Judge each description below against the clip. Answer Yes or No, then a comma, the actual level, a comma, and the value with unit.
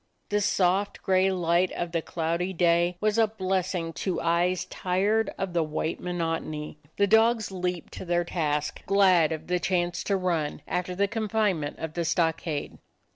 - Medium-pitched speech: Yes, medium, 180 Hz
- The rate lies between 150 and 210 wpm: Yes, average, 165 wpm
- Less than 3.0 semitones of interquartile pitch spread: Yes, narrow, 2.5 semitones